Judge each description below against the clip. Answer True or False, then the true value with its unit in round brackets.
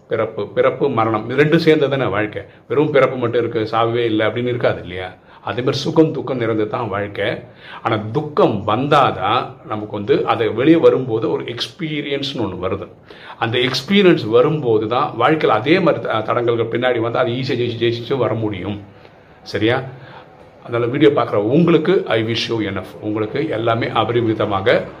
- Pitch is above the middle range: False (120 Hz)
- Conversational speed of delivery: False (150 wpm)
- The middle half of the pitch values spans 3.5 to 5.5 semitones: True (5.1 semitones)